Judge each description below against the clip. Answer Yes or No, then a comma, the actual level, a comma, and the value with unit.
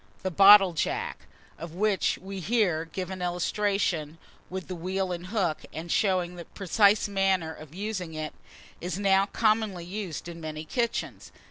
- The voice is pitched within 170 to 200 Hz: Yes, medium, 185 Hz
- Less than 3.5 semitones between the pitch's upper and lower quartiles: Yes, average, 3.0 semitones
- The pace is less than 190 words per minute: Yes, average, 155 wpm